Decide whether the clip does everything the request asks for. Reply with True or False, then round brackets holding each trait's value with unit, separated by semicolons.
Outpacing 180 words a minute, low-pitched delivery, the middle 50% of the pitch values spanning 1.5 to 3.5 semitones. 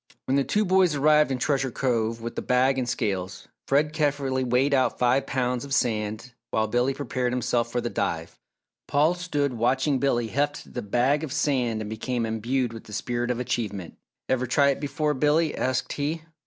True (190 wpm; 130 Hz; 3.2 semitones)